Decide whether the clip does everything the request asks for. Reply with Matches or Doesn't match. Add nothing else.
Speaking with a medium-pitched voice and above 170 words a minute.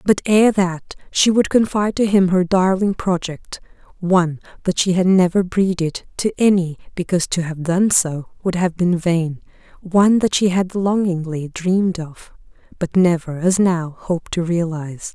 Doesn't match